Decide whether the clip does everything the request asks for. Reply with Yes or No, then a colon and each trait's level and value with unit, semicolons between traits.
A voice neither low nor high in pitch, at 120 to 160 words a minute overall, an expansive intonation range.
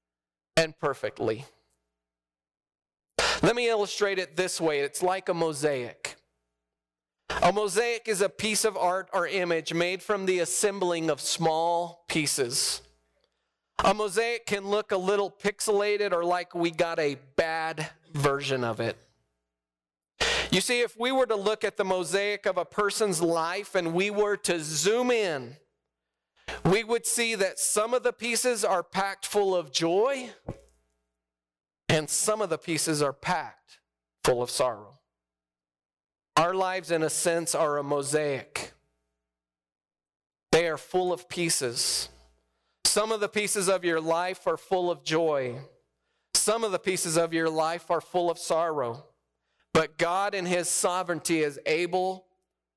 Yes: medium, 170 Hz; average, 145 wpm; wide, 8.2 semitones